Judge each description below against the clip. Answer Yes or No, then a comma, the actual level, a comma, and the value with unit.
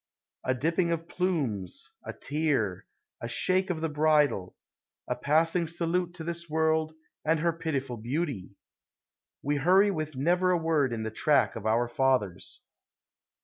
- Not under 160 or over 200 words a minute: No, average, 145 wpm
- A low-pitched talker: No, medium, 155 Hz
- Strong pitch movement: No, average, 4.6 semitones